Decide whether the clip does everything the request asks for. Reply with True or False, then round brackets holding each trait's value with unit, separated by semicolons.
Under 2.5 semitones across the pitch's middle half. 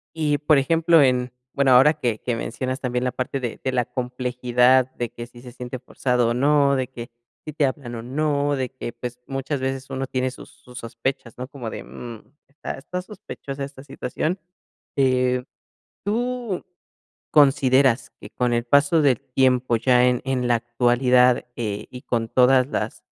True (2.1 semitones)